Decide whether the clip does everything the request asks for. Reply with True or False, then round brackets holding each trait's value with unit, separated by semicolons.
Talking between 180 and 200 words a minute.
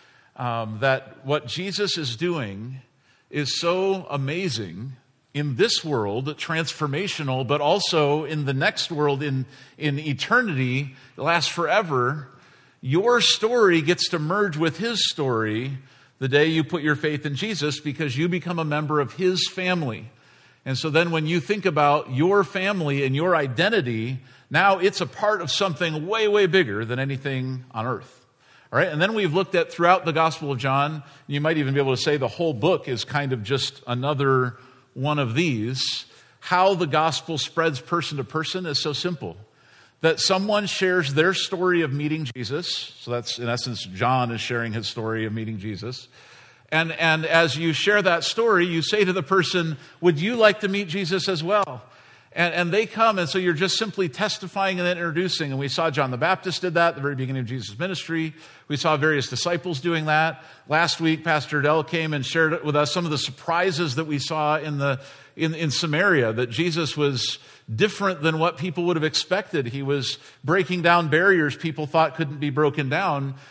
True (185 wpm)